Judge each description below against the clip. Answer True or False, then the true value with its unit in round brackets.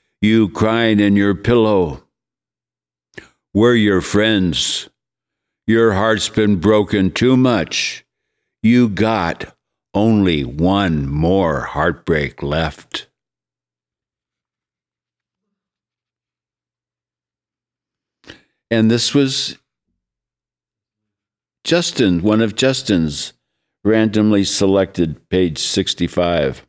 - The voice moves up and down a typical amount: False (7.5 semitones)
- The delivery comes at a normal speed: False (70 wpm)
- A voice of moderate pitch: False (100 Hz)